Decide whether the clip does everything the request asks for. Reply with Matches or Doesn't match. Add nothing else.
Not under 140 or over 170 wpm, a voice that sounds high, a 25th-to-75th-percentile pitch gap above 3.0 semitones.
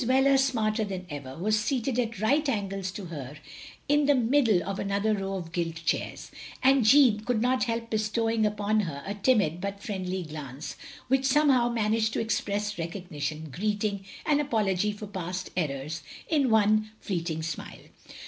Matches